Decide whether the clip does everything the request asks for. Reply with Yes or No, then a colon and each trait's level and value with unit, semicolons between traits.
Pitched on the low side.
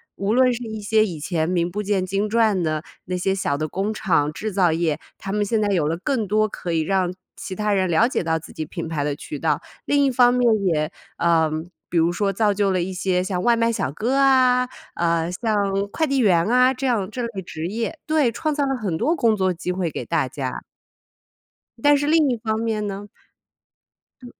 No: high, 200 Hz